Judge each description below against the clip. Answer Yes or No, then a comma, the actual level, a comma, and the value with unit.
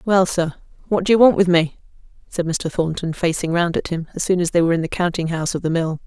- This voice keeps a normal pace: No, fast, 265 wpm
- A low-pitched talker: No, medium, 170 Hz